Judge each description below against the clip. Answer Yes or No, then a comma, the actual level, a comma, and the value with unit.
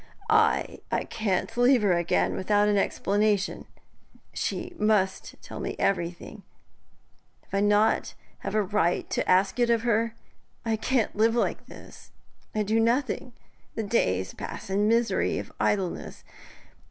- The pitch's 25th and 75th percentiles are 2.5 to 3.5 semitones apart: Yes, average, 2.9 semitones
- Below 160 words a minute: Yes, average, 140 wpm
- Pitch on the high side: Yes, high, 210 Hz